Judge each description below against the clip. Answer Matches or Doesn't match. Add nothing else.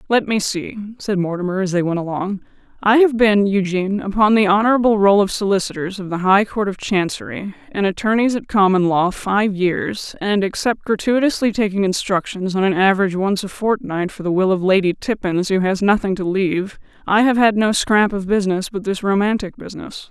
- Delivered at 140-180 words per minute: Doesn't match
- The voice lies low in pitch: Doesn't match